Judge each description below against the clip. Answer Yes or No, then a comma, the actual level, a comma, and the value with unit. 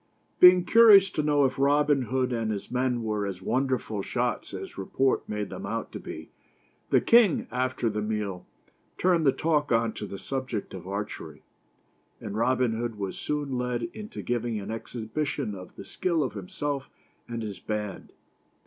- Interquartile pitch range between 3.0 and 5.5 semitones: Yes, average, 5.2 semitones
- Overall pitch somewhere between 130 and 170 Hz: No, low, 120 Hz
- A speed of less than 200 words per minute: Yes, average, 170 wpm